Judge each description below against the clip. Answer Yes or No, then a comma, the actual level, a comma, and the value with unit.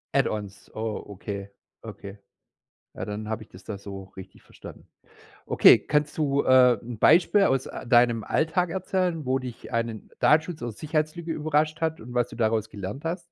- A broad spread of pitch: Yes, wide, 6.3 semitones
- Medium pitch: No, low, 125 Hz